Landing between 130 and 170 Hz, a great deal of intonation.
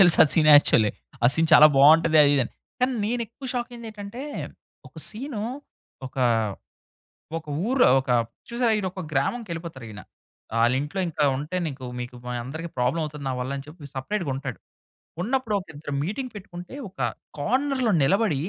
Yes: medium, 165 Hz; wide, 8.0 semitones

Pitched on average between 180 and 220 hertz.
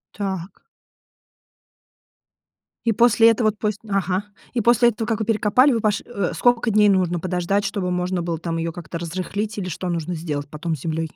Yes: high, 190 Hz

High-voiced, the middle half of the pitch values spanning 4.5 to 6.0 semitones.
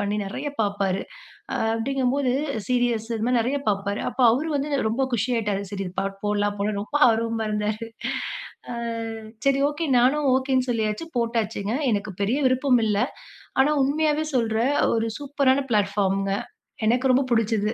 No: high, 230 Hz; average, 4.1 semitones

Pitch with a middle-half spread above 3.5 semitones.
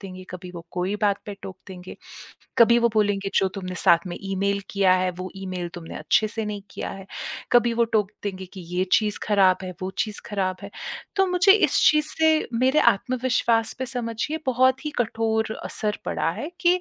Yes: average, 4.0 semitones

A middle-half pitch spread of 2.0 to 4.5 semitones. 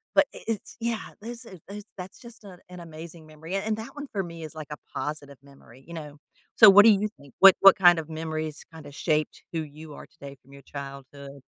No: average, 4.9 semitones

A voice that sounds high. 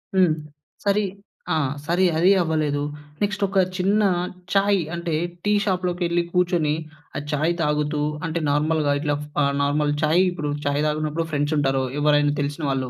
No: medium, 155 Hz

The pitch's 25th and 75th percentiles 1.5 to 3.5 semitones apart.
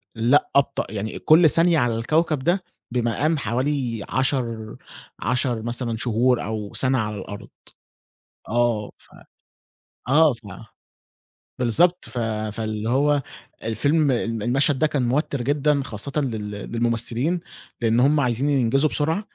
No: average, 4.3 semitones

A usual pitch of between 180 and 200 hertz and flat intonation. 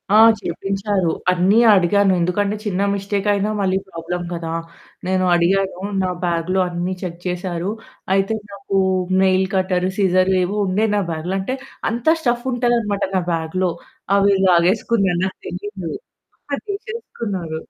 Yes: high, 190 Hz; narrow, 2.3 semitones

